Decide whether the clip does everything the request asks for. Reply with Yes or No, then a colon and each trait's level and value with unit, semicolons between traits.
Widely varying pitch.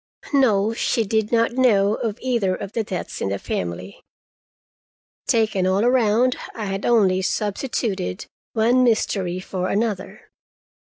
No: average, 3.6 semitones